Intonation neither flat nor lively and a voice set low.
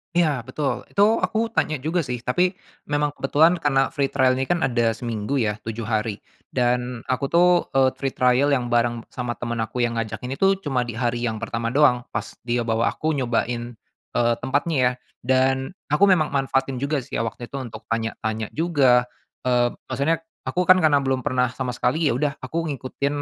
Yes: average, 3.5 semitones; low, 130 Hz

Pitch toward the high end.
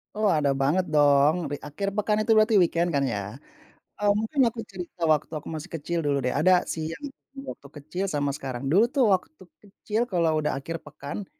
No: medium, 165 Hz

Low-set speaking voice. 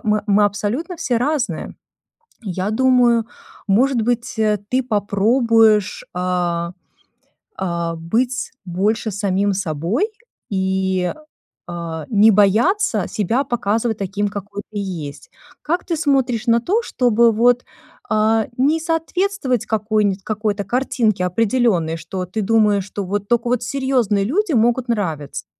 No: high, 215 Hz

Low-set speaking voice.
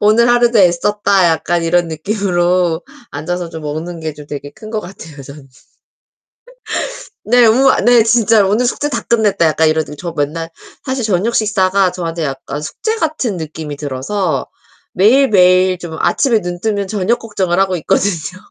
No: medium, 185 Hz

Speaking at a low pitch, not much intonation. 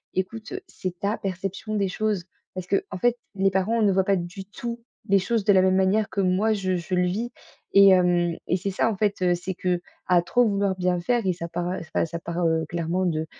No: high, 190 Hz; narrow, 2.2 semitones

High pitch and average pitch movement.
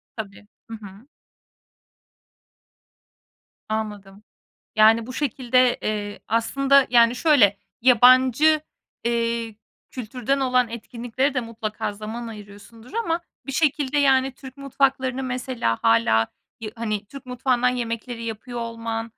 Yes: high, 235 Hz; average, 3.0 semitones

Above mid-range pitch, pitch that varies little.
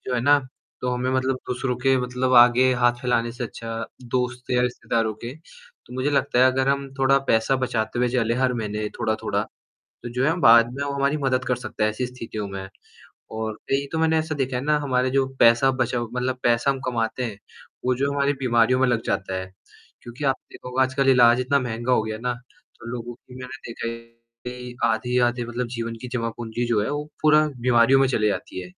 No: low, 125 Hz; narrow, 2.1 semitones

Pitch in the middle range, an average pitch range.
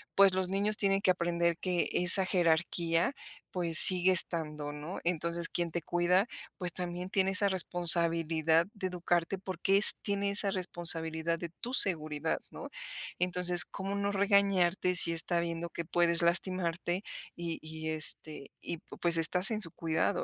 No: medium, 175 Hz; narrow, 2.1 semitones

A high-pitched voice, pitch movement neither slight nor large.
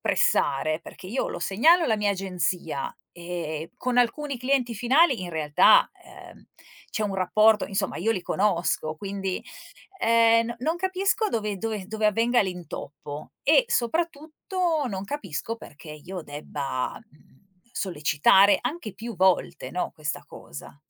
No: high, 205 Hz; wide, 5.7 semitones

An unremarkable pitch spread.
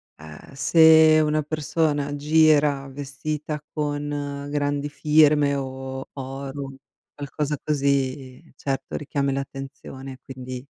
No: narrow, 1.7 semitones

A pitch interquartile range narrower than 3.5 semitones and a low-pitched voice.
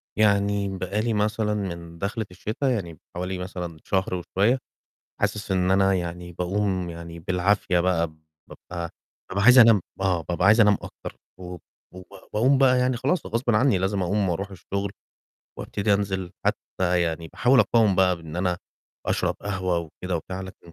Yes: average, 2.8 semitones; very low, 95 Hz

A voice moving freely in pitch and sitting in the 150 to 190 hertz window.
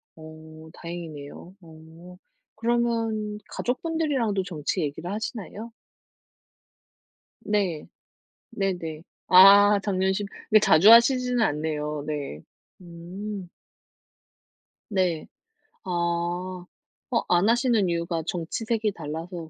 No: average, 5.0 semitones; medium, 185 Hz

